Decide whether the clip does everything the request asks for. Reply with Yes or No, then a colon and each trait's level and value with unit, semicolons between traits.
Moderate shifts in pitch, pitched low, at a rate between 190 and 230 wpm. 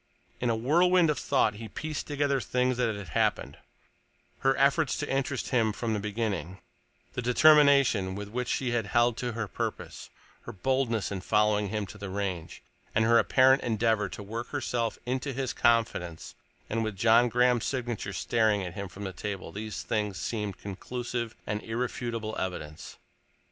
No: average, 3.5 semitones; low, 115 Hz; average, 165 wpm